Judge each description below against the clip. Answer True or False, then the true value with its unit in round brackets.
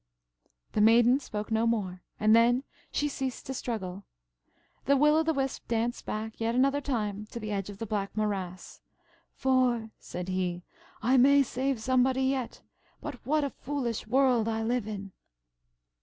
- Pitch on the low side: False (235 Hz)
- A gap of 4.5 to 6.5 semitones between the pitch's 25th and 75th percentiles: False (3.9 semitones)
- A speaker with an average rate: True (165 wpm)